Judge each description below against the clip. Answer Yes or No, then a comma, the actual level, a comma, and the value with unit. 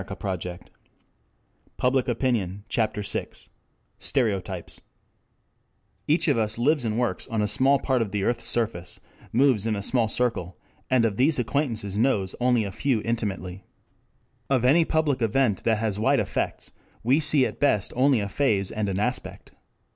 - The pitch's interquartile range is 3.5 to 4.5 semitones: Yes, average, 4.2 semitones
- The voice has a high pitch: No, low, 115 Hz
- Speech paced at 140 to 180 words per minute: Yes, average, 160 wpm